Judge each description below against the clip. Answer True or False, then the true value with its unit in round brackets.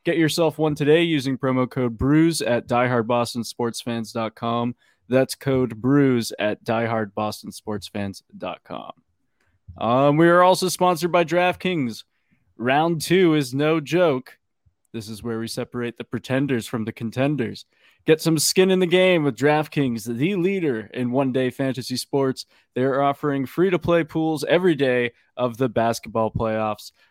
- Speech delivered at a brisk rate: False (135 wpm)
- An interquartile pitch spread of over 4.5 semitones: True (5.1 semitones)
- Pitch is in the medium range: False (130 Hz)